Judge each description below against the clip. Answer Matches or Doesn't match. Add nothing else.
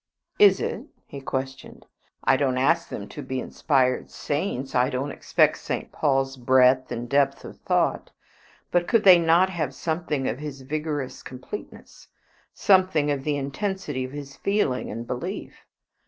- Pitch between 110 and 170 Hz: Matches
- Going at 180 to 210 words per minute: Doesn't match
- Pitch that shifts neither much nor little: Matches